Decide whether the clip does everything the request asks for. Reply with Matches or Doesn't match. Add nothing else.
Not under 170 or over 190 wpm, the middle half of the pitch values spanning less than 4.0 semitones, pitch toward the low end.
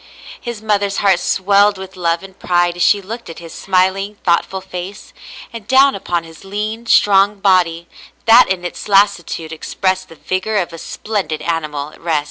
Doesn't match